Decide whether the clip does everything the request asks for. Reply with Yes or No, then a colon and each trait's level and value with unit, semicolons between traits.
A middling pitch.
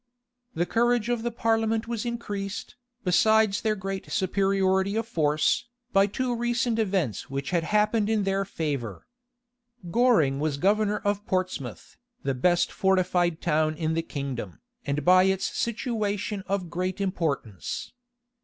No: high, 195 Hz